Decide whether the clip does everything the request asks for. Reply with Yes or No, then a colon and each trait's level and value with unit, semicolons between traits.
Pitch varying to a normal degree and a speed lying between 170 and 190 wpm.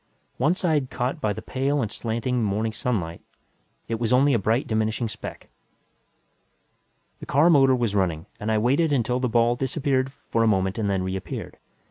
Yes: average, 3.6 semitones; average, 175 wpm